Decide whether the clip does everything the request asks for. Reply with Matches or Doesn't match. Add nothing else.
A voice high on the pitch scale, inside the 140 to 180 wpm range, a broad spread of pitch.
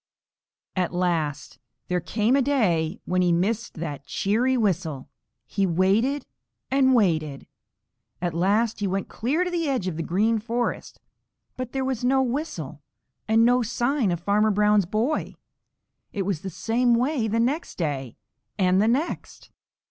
Matches